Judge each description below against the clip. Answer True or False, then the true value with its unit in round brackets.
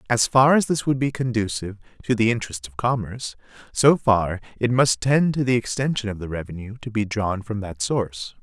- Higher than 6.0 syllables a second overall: False (5.6 syllables/s)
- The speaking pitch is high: False (110 Hz)